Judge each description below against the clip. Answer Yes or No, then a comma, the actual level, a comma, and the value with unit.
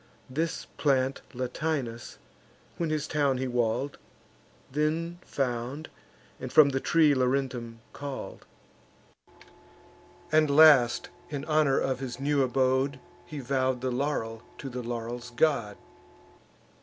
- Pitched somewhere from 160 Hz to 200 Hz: No, low, 135 Hz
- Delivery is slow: Yes, slow, 115 wpm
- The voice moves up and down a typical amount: Yes, average, 3.1 semitones